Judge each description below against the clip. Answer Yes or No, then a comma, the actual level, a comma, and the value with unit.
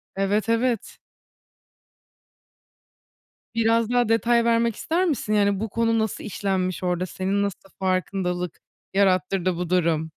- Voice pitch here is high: Yes, high, 200 Hz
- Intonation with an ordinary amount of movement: Yes, average, 3.7 semitones